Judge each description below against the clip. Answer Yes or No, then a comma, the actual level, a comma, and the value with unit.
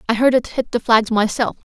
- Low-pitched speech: No, high, 235 Hz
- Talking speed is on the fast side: Yes, fast, 245 wpm